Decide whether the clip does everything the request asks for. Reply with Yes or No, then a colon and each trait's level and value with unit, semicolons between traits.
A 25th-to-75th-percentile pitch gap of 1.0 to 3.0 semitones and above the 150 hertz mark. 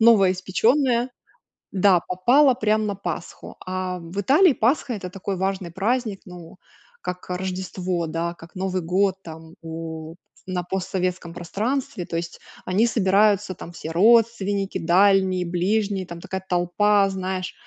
Yes: average, 2.7 semitones; high, 190 Hz